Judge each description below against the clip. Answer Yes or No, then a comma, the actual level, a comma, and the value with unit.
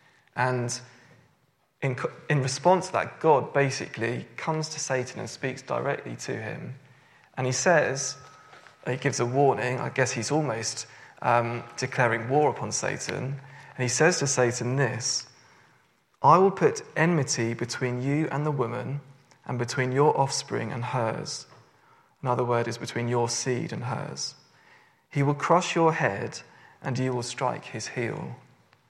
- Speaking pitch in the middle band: No, low, 130 Hz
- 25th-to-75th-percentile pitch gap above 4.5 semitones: No, average, 2.8 semitones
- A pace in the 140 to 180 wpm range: Yes, average, 150 wpm